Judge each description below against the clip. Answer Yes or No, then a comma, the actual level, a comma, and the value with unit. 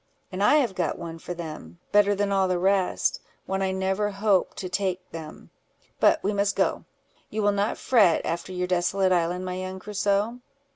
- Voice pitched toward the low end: No, high, 190 Hz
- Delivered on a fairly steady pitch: Yes, narrow, 2.1 semitones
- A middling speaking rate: Yes, average, 185 wpm